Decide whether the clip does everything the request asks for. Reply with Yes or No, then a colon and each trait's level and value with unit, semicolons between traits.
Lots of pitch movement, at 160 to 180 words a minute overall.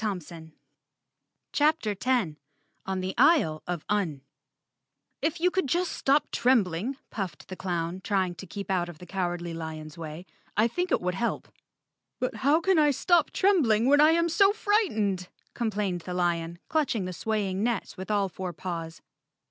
Yes: wide, 7.7 semitones; average, 165 wpm